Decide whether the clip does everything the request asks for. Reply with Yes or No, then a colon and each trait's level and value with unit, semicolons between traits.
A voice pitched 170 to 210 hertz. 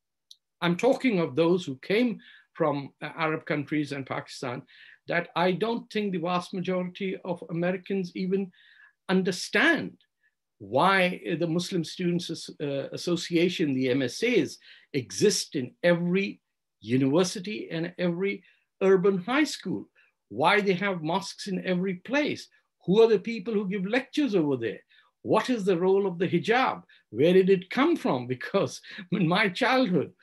Yes: medium, 185 Hz